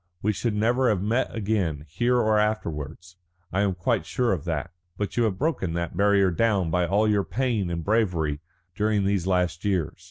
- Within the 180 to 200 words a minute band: Yes, average, 190 wpm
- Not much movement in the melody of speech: No, average, 4.0 semitones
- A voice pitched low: Yes, low, 100 Hz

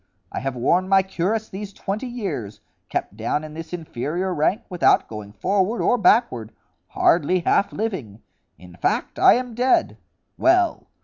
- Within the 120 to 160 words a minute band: Yes, average, 150 wpm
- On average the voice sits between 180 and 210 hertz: Yes, medium, 185 Hz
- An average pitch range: No, wide, 8.1 semitones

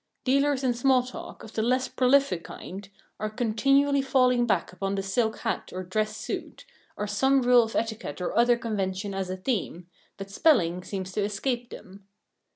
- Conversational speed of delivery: Yes, average, 175 wpm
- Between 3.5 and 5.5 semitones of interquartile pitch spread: Yes, average, 4.6 semitones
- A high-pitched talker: Yes, high, 220 Hz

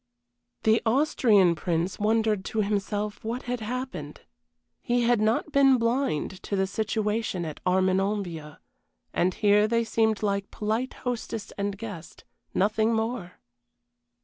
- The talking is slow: Yes, slow, 125 wpm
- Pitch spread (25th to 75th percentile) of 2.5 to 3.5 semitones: Yes, average, 3.1 semitones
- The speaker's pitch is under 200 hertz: No, high, 215 Hz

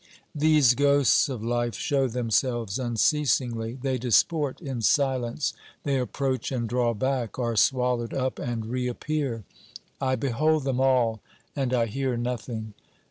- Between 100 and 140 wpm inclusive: Yes, slow, 135 wpm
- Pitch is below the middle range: Yes, low, 125 Hz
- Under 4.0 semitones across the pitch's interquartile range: Yes, narrow, 2.4 semitones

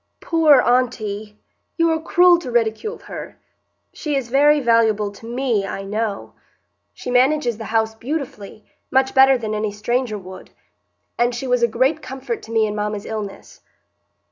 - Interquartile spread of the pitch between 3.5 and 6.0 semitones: Yes, average, 3.9 semitones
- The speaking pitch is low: No, high, 240 Hz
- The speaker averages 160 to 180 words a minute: No, average, 150 wpm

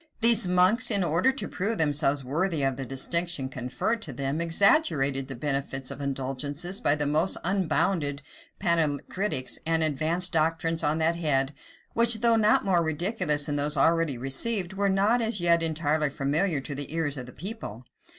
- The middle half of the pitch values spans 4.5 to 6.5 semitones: Yes, average, 5.1 semitones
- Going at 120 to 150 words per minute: No, average, 170 wpm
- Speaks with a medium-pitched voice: Yes, medium, 160 Hz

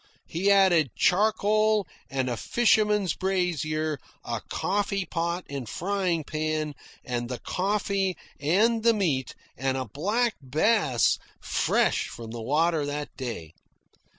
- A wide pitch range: Yes, wide, 6.4 semitones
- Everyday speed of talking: No, slow, 125 wpm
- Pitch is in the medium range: Yes, medium, 170 Hz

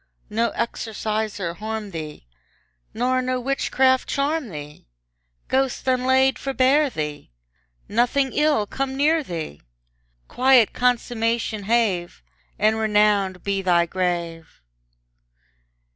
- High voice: Yes, high, 220 Hz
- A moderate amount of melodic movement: No, wide, 5.7 semitones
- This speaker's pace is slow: Yes, slow, 100 wpm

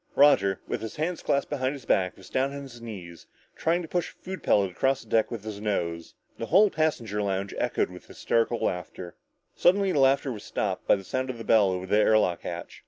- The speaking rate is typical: No, fast, 230 wpm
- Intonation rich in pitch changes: Yes, wide, 6.1 semitones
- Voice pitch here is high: No, low, 115 Hz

